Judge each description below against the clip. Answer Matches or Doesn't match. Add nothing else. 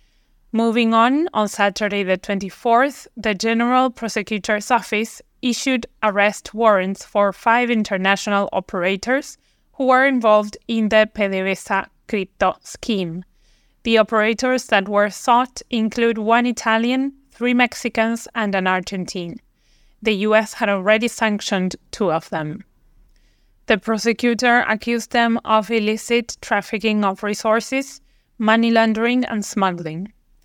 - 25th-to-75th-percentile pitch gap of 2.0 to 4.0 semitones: Matches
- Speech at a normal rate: Doesn't match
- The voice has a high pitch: Matches